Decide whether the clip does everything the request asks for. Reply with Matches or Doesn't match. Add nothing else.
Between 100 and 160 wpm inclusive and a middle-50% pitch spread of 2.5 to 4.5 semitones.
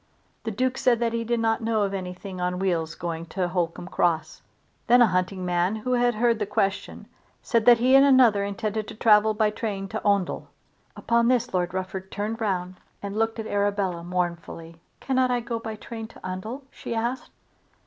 Doesn't match